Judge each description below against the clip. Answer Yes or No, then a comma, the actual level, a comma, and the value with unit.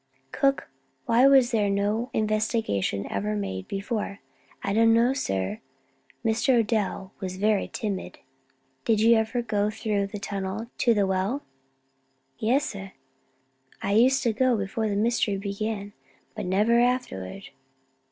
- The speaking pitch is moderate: No, high, 215 Hz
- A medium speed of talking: No, slow, 130 wpm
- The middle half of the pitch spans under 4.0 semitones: Yes, average, 2.9 semitones